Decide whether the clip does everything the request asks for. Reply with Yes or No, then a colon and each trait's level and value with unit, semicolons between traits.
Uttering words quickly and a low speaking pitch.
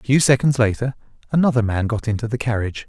Yes: fast, 210 wpm; low, 120 Hz